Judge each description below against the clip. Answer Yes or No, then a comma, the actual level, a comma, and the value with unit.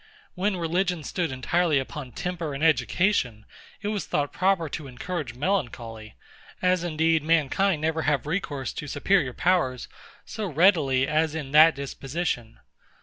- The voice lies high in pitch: No, medium, 155 Hz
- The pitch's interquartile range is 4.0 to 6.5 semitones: Yes, average, 4.8 semitones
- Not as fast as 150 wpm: Yes, average, 140 wpm